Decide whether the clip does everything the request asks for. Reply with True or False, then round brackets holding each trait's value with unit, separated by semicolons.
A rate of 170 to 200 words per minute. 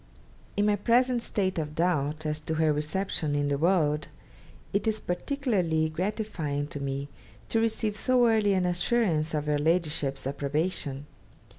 False (150 wpm)